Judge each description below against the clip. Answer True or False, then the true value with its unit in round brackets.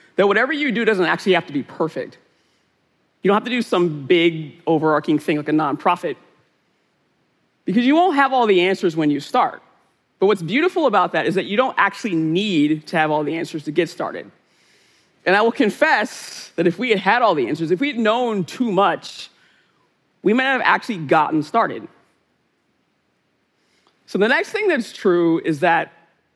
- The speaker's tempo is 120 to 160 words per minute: False (190 wpm)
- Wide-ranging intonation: True (6.6 semitones)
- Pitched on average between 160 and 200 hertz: True (185 Hz)